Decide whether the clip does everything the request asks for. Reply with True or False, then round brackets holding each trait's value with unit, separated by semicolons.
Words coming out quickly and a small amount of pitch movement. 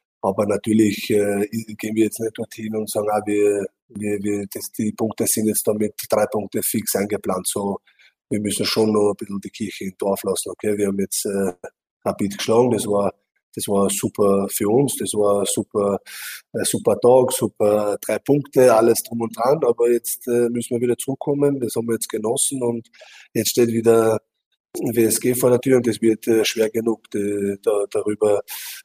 True (195 wpm; 2.1 semitones)